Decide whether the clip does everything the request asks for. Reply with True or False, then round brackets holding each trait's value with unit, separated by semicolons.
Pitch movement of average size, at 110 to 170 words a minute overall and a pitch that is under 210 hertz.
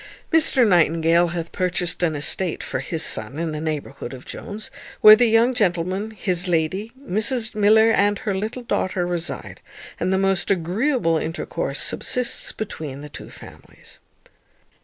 True (4.7 semitones; 150 wpm; 185 Hz)